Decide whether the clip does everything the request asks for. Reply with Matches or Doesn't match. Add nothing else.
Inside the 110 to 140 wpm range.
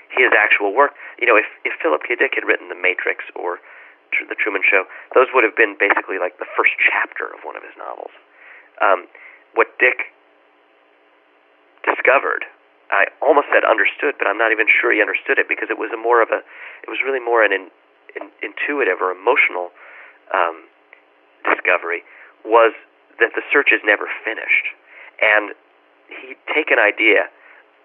Doesn't match